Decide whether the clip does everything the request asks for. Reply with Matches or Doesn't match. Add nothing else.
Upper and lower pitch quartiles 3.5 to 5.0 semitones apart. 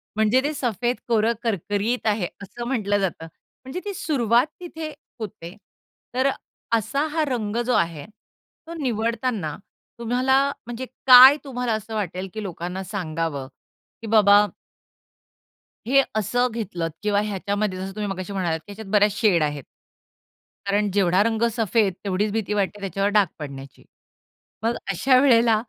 Matches